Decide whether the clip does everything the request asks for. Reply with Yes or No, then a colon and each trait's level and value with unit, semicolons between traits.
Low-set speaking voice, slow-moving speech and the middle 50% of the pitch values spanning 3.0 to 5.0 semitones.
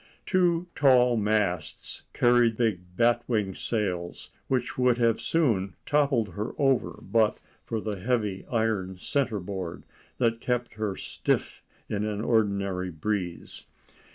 Yes: low, 110 Hz; slow, 125 wpm; average, 3.8 semitones